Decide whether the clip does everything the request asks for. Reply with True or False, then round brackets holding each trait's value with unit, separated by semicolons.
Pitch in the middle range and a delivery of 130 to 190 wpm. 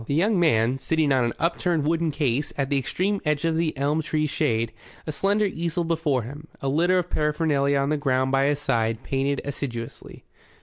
False (145 Hz; 200 wpm)